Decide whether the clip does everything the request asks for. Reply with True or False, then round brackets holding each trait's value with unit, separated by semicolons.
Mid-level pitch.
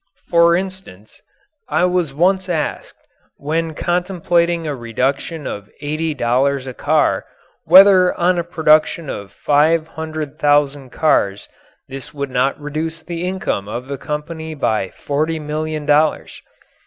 True (155 Hz)